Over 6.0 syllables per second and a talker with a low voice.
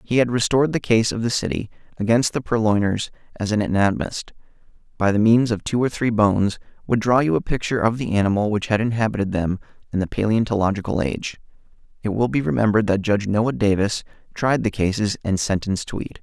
Yes: 6.2 syllables/s; low, 105 Hz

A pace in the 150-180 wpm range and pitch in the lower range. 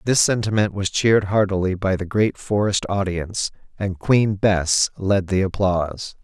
Yes: average, 155 wpm; low, 100 Hz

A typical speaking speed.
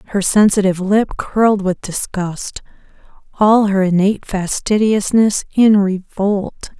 No: slow, 105 wpm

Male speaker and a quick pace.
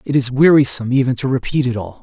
Yes: male; fast, 235 wpm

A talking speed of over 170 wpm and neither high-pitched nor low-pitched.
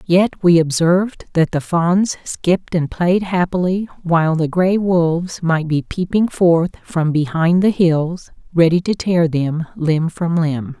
No: average, 160 wpm; medium, 170 Hz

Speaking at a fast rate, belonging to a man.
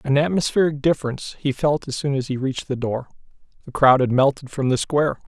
Yes: fast, 210 wpm; male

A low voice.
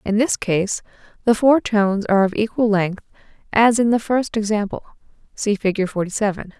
No: high, 210 Hz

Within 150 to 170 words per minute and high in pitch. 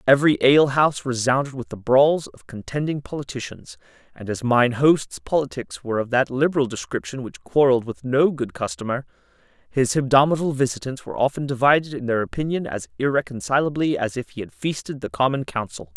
No: average, 165 wpm; low, 130 Hz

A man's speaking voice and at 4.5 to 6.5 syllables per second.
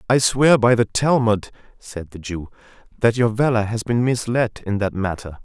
Yes: male; 4.7 syllables/s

